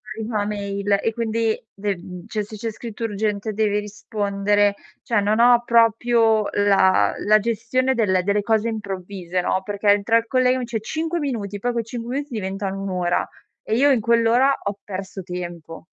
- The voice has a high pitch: Yes, high, 210 Hz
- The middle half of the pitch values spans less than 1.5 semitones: No, average, 2.7 semitones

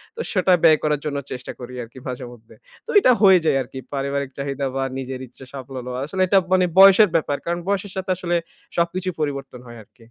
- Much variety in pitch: Yes, wide, 5.8 semitones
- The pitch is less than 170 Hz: Yes, medium, 140 Hz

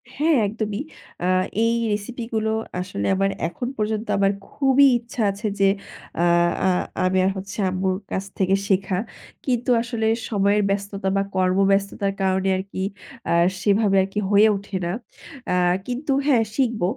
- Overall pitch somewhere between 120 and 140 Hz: No, high, 200 Hz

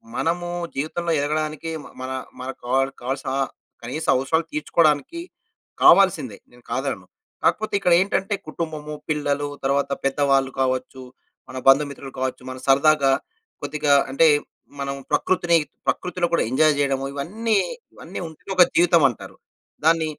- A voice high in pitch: No, medium, 145 Hz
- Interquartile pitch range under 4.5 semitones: Yes, average, 3.5 semitones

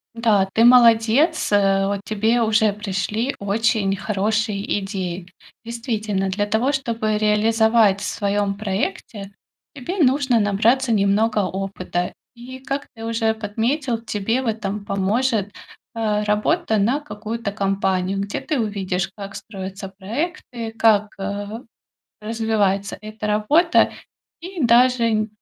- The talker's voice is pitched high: Yes, high, 215 Hz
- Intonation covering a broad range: No, narrow, 2.6 semitones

